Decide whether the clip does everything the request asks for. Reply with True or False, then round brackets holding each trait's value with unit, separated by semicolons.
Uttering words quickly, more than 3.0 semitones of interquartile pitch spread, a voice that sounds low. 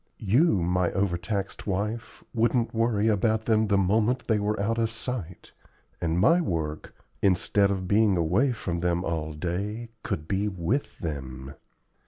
False (150 wpm; 4.3 semitones; 100 Hz)